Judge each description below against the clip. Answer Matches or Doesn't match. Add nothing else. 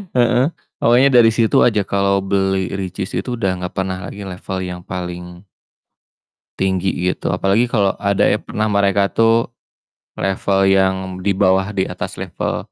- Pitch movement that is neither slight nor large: Doesn't match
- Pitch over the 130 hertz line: Doesn't match